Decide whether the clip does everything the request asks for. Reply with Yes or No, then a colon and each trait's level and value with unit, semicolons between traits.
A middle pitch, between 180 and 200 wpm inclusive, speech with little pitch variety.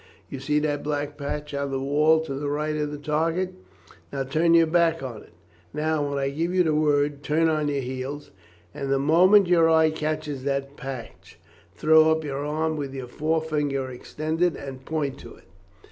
Yes: medium, 150 Hz; average, 190 wpm; narrow, 2.3 semitones